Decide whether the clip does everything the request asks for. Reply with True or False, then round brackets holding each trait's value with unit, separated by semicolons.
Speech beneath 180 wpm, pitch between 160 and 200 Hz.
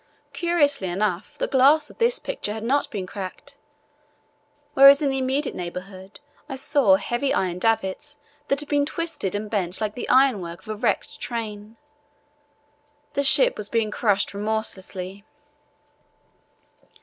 False (140 wpm; 225 Hz)